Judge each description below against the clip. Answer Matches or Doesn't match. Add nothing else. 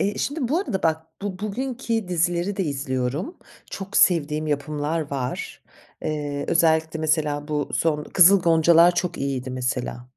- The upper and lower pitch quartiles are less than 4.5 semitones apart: Matches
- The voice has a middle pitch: Matches